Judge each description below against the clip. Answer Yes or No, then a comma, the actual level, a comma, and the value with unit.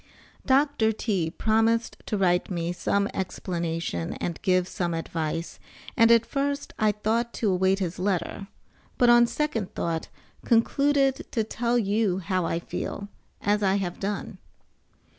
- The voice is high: Yes, high, 200 Hz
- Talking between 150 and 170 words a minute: No, average, 140 wpm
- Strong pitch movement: No, average, 4.5 semitones